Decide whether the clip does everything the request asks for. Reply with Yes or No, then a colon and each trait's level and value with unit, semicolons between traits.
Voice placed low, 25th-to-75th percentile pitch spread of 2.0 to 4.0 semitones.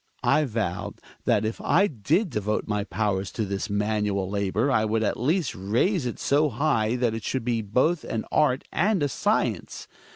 No: low, 115 Hz; wide, 5.5 semitones